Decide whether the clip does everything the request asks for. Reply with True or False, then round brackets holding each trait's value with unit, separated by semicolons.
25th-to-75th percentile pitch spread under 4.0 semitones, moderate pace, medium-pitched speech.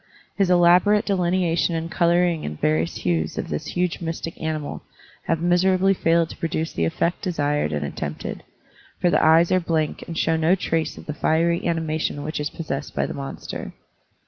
True (2.6 semitones; 175 wpm; 165 Hz)